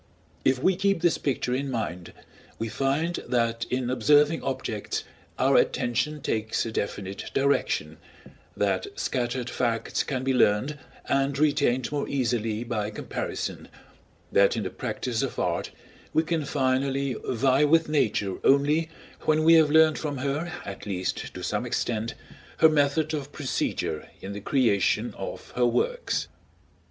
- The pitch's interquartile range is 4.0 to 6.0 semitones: Yes, average, 4.4 semitones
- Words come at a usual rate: Yes, average, 145 wpm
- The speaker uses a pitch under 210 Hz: Yes, low, 135 Hz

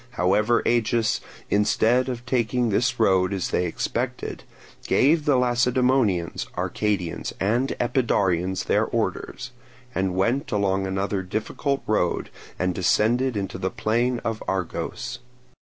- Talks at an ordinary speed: No, slow, 120 wpm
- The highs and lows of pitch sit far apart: No, average, 4.5 semitones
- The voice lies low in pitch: Yes, low, 110 Hz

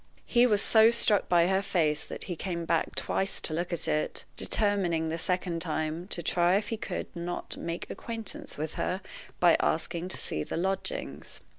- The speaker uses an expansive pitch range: No, average, 3.2 semitones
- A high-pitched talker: No, medium, 175 Hz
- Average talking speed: Yes, average, 185 wpm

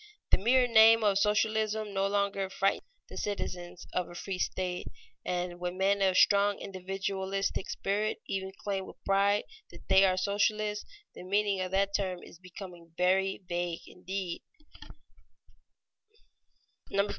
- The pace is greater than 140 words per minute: No, slow, 135 wpm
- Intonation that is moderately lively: No, narrow, 1.7 semitones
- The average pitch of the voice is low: No, high, 195 Hz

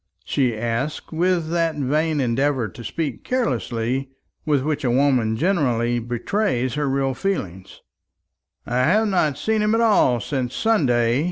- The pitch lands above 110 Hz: Yes, low, 135 Hz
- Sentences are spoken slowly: No, average, 145 wpm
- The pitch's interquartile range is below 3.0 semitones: No, wide, 5.4 semitones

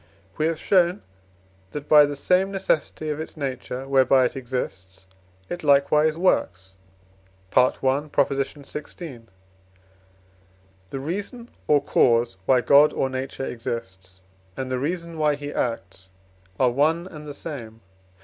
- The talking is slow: Yes, slow, 130 wpm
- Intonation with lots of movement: No, average, 3.7 semitones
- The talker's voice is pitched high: No, medium, 140 Hz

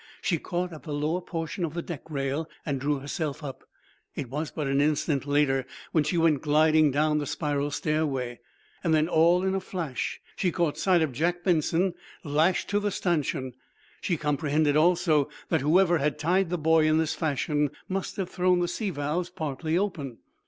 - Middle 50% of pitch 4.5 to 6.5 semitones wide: No, average, 3.1 semitones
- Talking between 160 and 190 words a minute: Yes, average, 185 wpm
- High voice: No, medium, 155 Hz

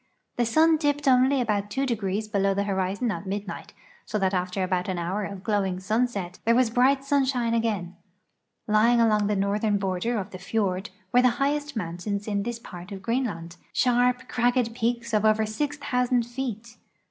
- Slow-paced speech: No, average, 175 wpm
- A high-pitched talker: Yes, high, 220 Hz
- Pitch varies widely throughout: No, average, 3.9 semitones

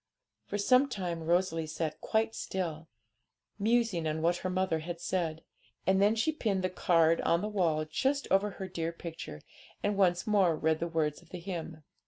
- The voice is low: No, medium, 175 Hz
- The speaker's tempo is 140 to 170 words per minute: No, average, 185 wpm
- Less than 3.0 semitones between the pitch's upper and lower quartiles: No, average, 3.5 semitones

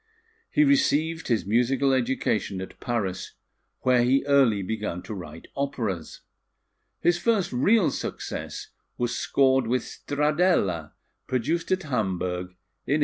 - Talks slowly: Yes, slow, 125 wpm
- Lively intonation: Yes, wide, 6.4 semitones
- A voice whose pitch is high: No, low, 125 Hz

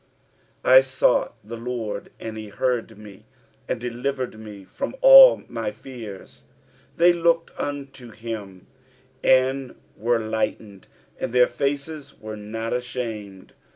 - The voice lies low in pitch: Yes, low, 120 Hz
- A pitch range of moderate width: Yes, average, 3.8 semitones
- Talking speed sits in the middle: No, slow, 130 wpm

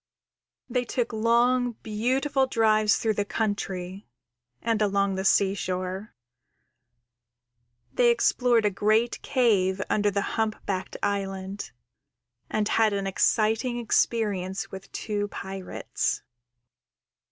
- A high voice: Yes, high, 210 Hz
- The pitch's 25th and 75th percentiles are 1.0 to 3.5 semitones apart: Yes, average, 3.0 semitones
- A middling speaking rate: No, slow, 105 wpm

